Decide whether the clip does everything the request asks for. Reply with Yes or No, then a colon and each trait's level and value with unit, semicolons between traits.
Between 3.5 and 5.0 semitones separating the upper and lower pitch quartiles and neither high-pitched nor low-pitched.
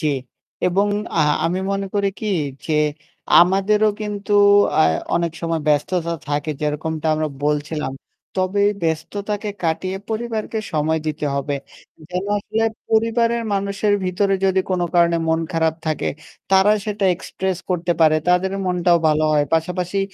Yes: average, 3.9 semitones; medium, 180 Hz